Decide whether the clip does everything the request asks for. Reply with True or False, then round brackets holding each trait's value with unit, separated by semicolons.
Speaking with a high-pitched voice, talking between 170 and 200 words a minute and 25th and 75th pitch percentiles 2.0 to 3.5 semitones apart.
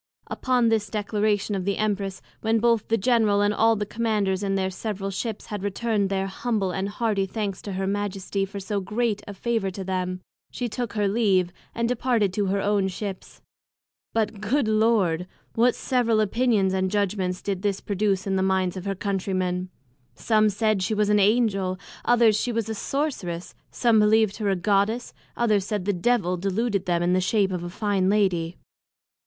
True (205 Hz; 190 wpm; 2.5 semitones)